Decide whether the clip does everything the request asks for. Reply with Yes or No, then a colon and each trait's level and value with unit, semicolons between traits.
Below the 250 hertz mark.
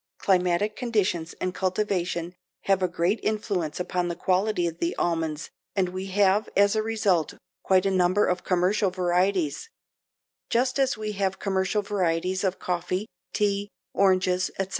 Yes: medium, 185 Hz